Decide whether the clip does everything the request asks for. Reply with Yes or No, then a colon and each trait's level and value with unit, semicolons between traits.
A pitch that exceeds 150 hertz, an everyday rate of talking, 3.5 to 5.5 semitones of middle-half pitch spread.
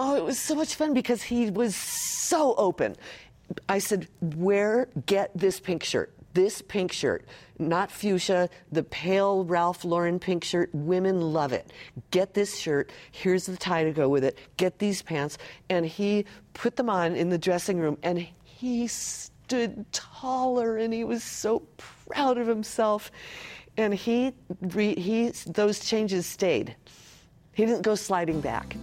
Yes: high, 190 Hz; average, 160 wpm; average, 4.2 semitones